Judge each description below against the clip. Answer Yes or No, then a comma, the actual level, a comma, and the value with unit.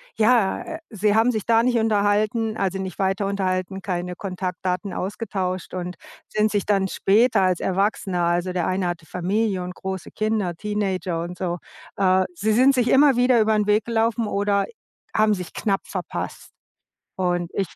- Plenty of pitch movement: No, average, 2.9 semitones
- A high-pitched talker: Yes, high, 195 Hz